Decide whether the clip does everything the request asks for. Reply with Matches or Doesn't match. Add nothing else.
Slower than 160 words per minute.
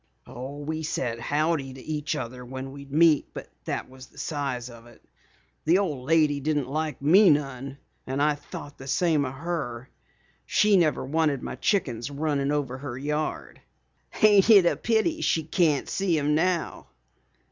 Doesn't match